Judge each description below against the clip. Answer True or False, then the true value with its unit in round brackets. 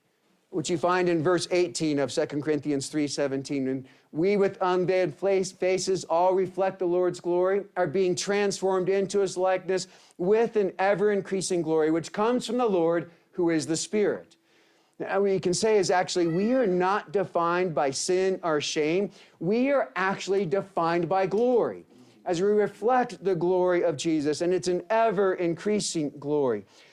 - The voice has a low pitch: False (185 Hz)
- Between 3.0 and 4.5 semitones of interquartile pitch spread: False (2.6 semitones)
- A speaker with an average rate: True (165 wpm)